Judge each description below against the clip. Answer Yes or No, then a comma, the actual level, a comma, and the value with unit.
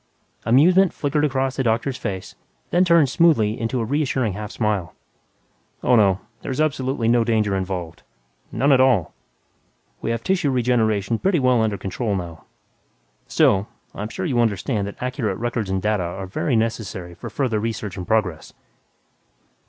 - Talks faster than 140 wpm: Yes, average, 150 wpm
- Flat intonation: No, average, 4.7 semitones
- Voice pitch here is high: No, low, 115 Hz